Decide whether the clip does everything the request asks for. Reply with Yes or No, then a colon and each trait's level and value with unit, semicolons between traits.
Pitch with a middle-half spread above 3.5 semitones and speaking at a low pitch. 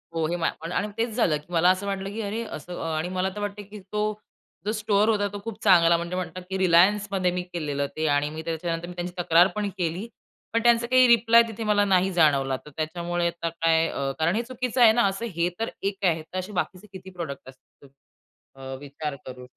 No: average, 4.0 semitones; medium, 185 Hz